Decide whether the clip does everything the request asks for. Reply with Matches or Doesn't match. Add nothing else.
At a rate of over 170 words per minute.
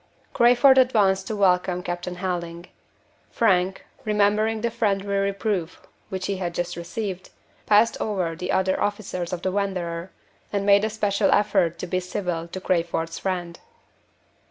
Doesn't match